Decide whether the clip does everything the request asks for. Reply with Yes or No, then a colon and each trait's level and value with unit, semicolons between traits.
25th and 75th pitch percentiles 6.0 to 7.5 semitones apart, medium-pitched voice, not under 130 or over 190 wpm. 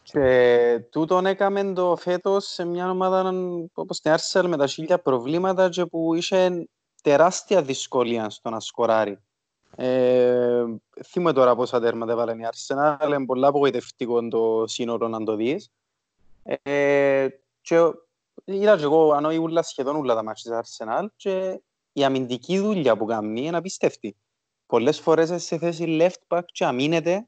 Yes: wide, 6.4 semitones; medium, 145 Hz; average, 145 wpm